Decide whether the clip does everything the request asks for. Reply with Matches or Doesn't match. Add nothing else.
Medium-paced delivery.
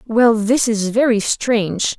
Matches